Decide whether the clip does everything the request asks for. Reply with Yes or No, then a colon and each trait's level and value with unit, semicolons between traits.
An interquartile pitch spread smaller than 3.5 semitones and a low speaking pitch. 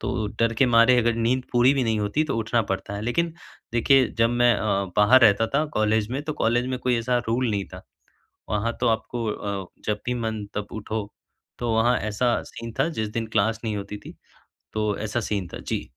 Yes: narrow, 2.4 semitones; low, 115 Hz